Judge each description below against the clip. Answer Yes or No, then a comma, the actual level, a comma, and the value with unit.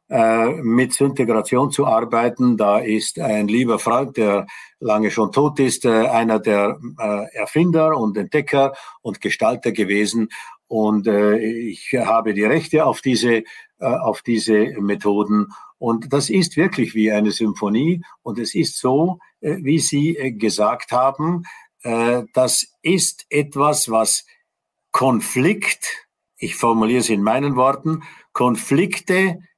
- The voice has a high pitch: No, low, 120 Hz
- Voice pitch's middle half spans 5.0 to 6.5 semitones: Yes, wide, 5.4 semitones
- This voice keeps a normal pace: No, slow, 120 wpm